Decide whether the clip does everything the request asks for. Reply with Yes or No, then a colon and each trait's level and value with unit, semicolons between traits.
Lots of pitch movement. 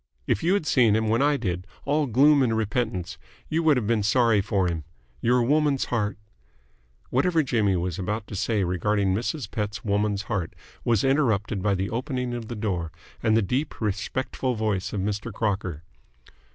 No: average, 4.3 semitones